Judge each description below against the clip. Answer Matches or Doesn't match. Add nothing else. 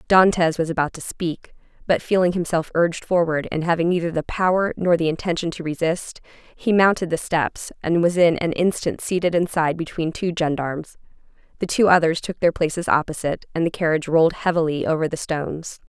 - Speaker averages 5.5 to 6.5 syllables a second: Matches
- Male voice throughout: Doesn't match